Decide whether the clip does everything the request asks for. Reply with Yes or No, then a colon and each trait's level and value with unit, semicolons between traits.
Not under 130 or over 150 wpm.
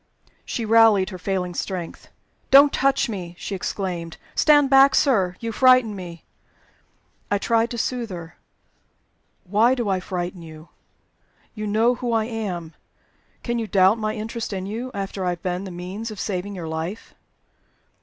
No: average, 160 wpm